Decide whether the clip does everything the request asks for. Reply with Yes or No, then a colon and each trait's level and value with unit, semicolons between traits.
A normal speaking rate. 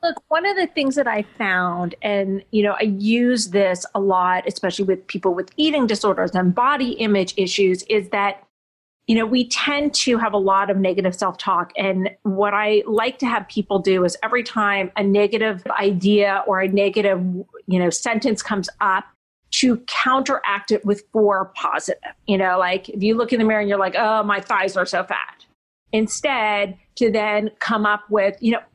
Yes: average, 195 wpm